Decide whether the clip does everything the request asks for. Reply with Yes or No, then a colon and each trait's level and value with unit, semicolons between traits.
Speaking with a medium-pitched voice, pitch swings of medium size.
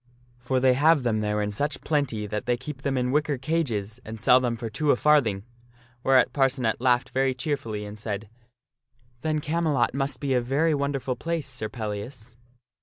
No: low, 125 Hz; average, 4.2 semitones